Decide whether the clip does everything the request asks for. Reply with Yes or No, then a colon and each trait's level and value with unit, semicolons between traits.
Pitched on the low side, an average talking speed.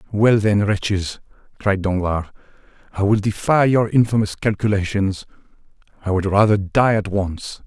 No: low, 100 Hz; slow, 125 wpm